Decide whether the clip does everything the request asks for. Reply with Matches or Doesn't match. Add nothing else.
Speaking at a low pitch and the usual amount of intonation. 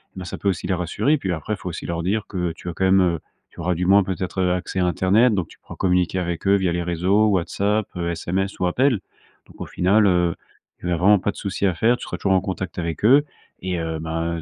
Doesn't match